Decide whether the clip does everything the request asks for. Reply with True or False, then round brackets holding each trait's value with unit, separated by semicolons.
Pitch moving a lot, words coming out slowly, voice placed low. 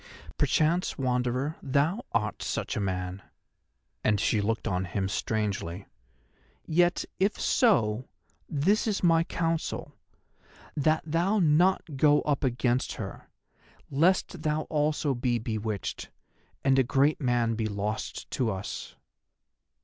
True (6.7 semitones; 120 wpm; 130 Hz)